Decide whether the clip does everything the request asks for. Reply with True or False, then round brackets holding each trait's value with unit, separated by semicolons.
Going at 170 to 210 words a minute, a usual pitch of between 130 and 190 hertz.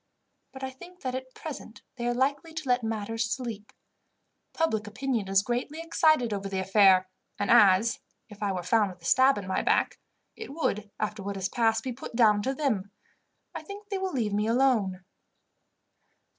False (185 wpm; 230 Hz)